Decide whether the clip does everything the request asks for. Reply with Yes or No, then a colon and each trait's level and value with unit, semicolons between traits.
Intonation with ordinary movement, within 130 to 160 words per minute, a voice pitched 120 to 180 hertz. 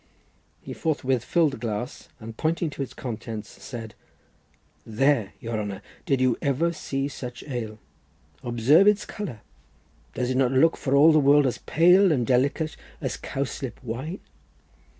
Yes: average, 4.6 semitones; average, 150 wpm; low, 135 Hz